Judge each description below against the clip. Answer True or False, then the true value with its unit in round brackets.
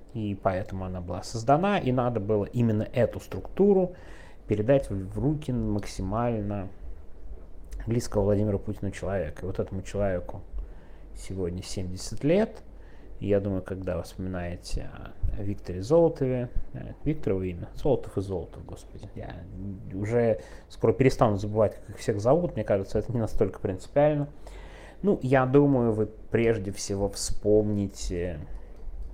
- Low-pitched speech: True (100 Hz)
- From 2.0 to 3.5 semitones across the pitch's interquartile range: False (4.1 semitones)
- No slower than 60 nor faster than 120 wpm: False (130 wpm)